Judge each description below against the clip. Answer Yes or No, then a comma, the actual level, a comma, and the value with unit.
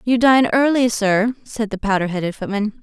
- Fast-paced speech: No, average, 190 wpm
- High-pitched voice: Yes, high, 220 Hz